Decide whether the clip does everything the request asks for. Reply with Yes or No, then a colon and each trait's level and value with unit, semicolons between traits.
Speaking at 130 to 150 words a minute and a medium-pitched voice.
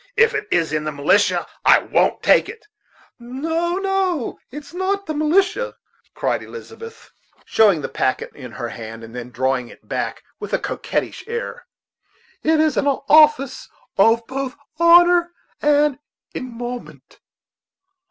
No: average, 145 wpm; very high, 290 Hz